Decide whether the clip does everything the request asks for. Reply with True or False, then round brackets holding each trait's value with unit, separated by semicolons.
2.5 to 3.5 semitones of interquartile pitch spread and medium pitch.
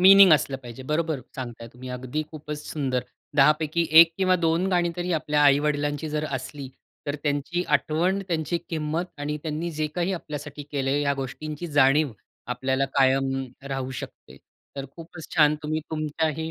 True (3.0 semitones; 150 Hz)